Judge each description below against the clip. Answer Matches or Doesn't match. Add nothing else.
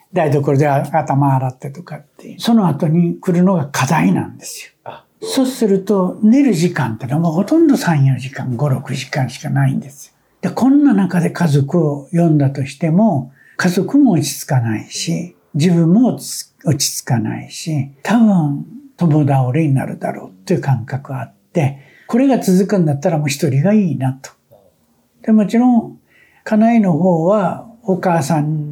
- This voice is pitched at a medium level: Matches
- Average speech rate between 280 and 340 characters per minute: Matches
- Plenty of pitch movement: Matches